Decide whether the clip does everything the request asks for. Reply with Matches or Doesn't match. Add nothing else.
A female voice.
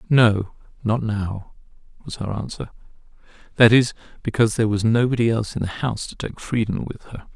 Doesn't match